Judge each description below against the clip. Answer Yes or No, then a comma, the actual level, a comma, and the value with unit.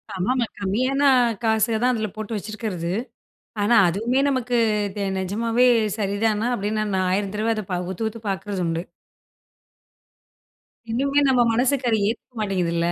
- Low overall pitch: No, high, 215 Hz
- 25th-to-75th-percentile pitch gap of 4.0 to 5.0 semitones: No, average, 3.5 semitones